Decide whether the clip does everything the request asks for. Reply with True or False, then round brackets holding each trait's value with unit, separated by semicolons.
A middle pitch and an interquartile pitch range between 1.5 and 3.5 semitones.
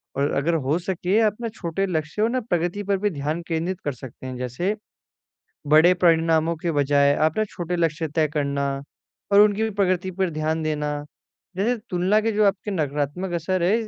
False (170 Hz; 4.2 semitones)